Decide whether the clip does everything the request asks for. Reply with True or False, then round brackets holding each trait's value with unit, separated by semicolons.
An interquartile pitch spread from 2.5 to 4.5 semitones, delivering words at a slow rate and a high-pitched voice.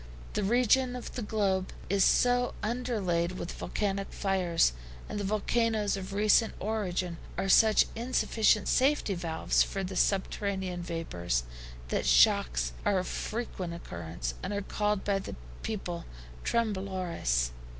True (3.8 semitones; 130 wpm; 195 Hz)